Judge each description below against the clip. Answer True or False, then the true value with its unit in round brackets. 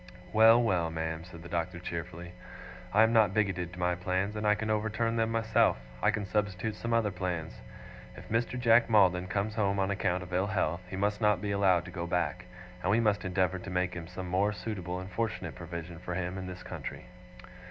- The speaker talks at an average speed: False (210 wpm)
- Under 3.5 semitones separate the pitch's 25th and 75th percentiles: True (3.1 semitones)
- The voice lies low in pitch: True (95 Hz)